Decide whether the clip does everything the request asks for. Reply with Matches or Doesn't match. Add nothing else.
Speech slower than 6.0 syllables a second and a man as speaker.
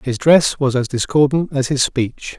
Matches